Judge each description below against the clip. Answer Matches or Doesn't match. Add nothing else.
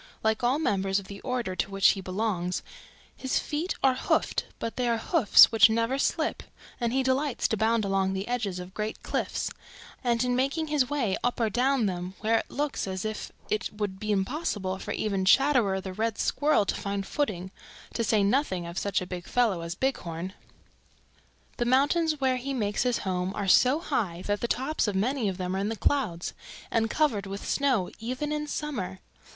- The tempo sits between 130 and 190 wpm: Doesn't match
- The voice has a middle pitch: Doesn't match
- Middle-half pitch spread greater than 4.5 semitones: Matches